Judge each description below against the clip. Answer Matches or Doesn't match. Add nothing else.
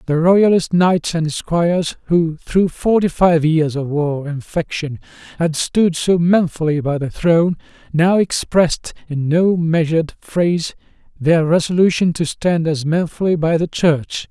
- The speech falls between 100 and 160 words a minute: Matches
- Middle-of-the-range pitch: Matches